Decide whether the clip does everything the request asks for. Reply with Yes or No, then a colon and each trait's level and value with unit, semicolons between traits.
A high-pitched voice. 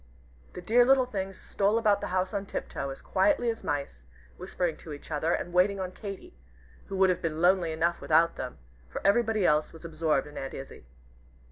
No: medium, 180 Hz